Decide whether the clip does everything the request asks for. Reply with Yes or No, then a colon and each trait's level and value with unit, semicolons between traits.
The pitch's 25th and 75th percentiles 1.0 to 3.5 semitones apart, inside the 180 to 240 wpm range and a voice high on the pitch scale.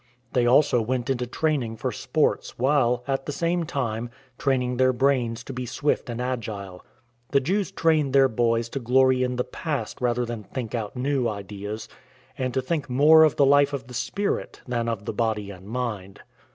No: average, 3.1 semitones; average, 190 wpm; low, 125 Hz